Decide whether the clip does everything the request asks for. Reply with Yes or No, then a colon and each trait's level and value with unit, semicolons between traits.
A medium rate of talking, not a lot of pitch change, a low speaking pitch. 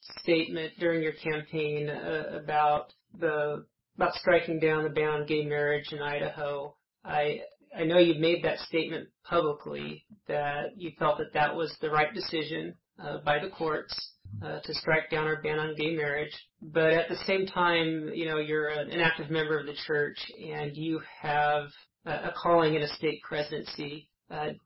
No: average, 175 wpm; narrow, 1.5 semitones; medium, 155 Hz